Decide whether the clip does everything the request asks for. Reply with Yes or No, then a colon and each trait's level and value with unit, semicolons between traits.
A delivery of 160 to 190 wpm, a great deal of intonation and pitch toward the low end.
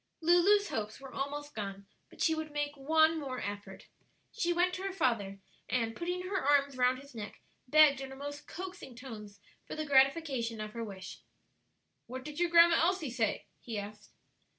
No: average, 180 wpm; wide, 6.1 semitones; very high, 275 Hz